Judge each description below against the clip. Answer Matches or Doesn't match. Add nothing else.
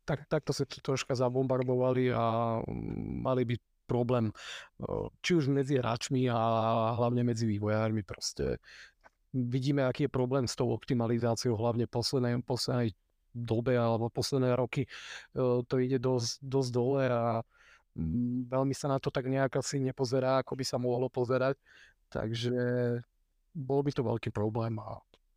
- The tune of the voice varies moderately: Doesn't match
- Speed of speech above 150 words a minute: Doesn't match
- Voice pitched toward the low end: Matches